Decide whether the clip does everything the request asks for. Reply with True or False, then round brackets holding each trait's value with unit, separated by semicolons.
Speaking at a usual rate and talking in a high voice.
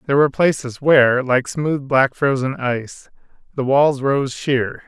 False (160 wpm; 135 Hz)